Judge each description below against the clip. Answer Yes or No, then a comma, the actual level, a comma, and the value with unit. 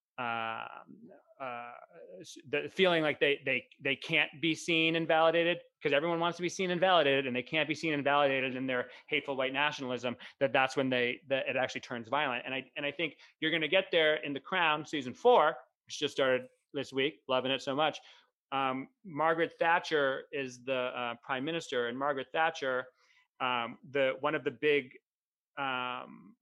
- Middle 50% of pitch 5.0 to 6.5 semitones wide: No, average, 3.8 semitones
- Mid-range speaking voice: Yes, medium, 145 Hz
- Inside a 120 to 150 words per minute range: No, average, 190 wpm